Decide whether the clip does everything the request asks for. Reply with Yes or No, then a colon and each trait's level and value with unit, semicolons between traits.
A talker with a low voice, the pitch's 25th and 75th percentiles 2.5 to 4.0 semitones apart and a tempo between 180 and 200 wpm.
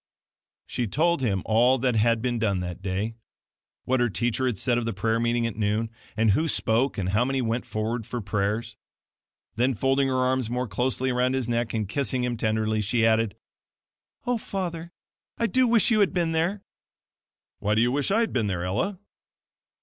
Yes: low, 120 Hz; average, 3.4 semitones; average, 195 wpm